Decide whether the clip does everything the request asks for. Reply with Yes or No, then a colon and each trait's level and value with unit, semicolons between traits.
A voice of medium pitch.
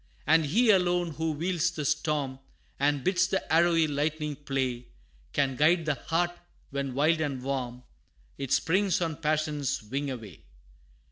Yes: medium, 150 Hz